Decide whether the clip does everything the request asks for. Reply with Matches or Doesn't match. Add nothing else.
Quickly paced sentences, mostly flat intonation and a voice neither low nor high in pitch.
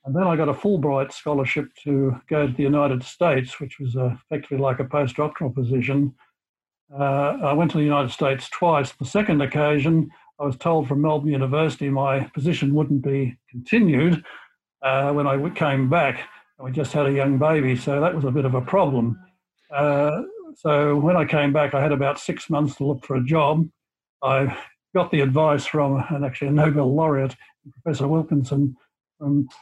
Doesn't match